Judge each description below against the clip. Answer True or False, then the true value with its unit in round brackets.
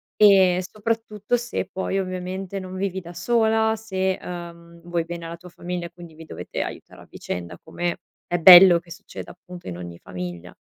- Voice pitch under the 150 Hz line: False (180 Hz)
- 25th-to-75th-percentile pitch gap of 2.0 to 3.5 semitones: True (2.3 semitones)